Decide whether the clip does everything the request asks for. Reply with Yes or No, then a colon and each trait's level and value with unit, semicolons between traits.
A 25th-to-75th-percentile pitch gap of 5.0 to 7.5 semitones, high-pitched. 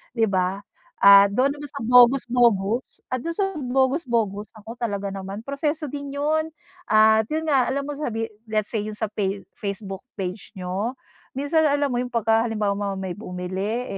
Yes: wide, 5.4 semitones; high, 225 Hz